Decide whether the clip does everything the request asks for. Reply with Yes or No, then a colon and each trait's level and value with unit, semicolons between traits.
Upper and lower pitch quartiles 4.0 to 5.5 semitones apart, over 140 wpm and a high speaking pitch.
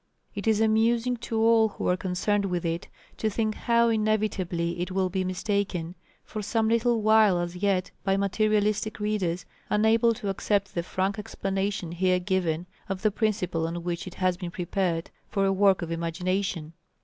No: average, 3.2 semitones; average, 175 wpm; high, 195 Hz